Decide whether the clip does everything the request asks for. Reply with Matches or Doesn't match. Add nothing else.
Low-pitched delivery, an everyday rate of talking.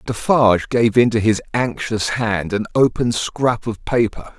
Matches